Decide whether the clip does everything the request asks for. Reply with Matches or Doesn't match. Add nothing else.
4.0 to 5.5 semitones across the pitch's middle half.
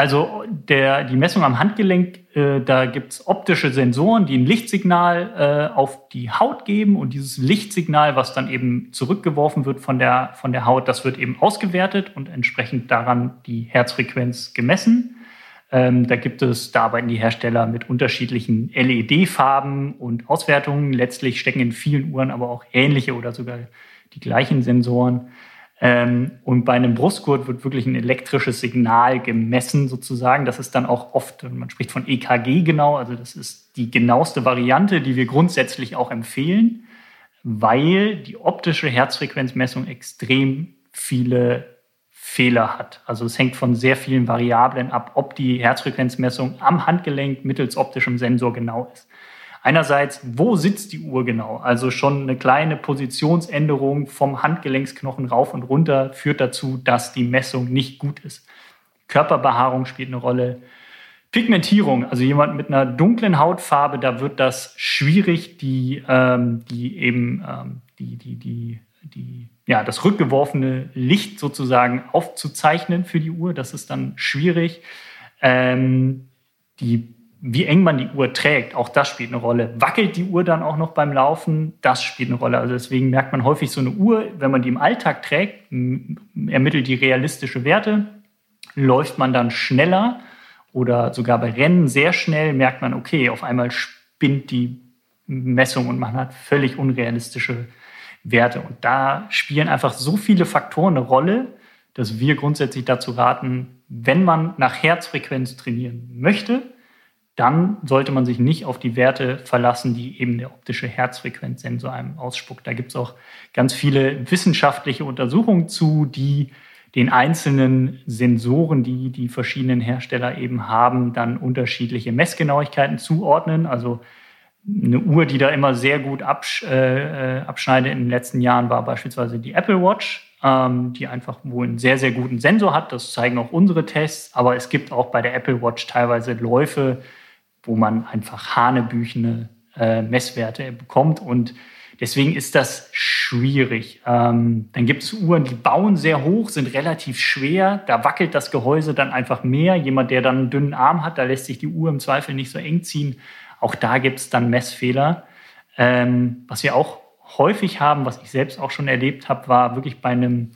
Doesn't match